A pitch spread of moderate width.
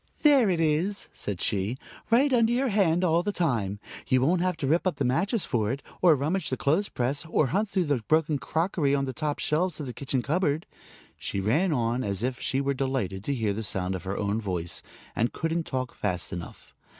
No: wide, 7.0 semitones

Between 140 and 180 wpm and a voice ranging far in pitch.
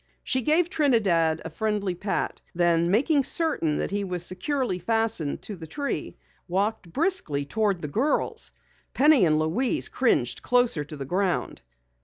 Yes: average, 150 wpm; wide, 7.3 semitones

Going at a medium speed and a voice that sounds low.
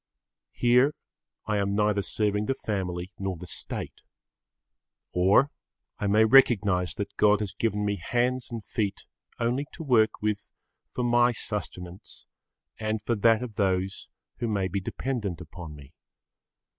Yes: average, 145 wpm; low, 105 Hz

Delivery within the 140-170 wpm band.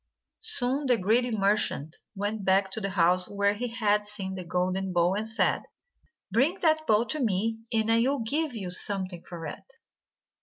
No: average, 180 wpm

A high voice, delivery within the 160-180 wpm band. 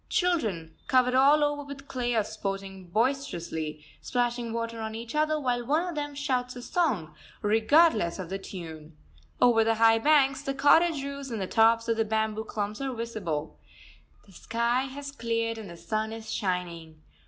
Yes: high, 230 Hz; average, 175 wpm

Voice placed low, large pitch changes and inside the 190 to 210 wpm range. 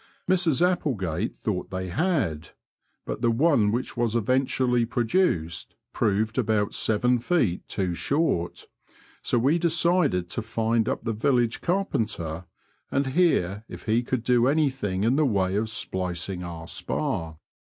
No: low, 115 Hz; wide, 6.2 semitones; average, 140 wpm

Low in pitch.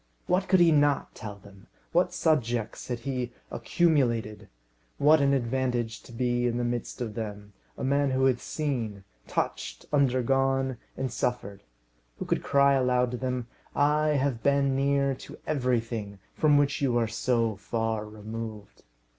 Yes: low, 125 Hz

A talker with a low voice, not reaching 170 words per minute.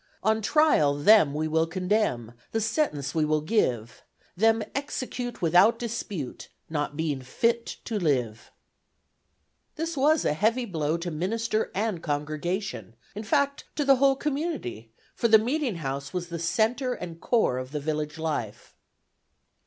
No: medium, 180 Hz; average, 145 wpm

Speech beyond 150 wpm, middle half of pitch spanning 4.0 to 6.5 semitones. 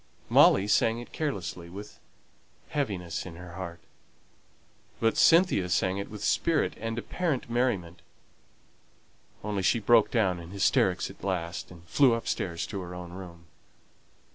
No: average, 140 wpm; average, 4.8 semitones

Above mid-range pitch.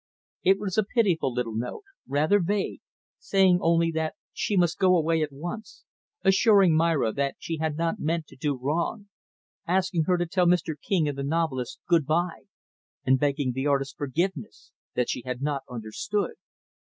No: medium, 165 Hz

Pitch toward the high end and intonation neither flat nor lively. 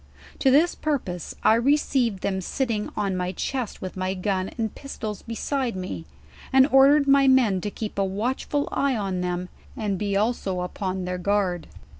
No: high, 210 Hz; wide, 5.9 semitones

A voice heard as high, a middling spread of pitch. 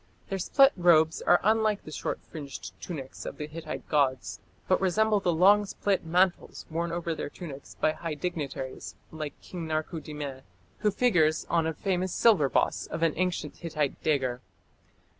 No: medium, 165 Hz; average, 3.4 semitones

